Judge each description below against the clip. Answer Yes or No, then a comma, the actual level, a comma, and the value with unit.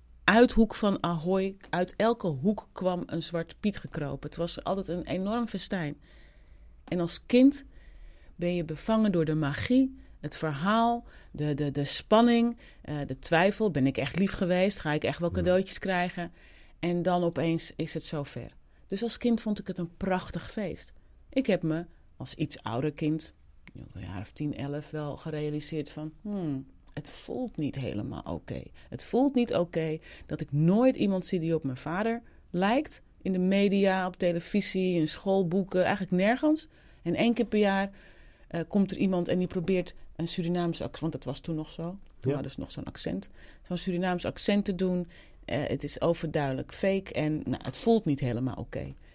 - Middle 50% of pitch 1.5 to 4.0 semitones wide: No, average, 4.6 semitones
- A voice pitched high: No, medium, 175 Hz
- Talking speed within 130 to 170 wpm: No, average, 185 wpm